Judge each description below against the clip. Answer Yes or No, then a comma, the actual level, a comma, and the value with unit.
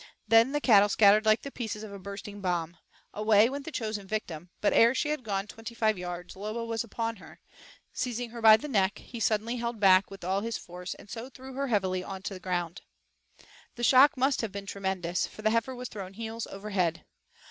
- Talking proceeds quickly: Yes, fast, 215 wpm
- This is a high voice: Yes, high, 215 Hz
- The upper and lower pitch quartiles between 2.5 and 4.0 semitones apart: Yes, average, 3.2 semitones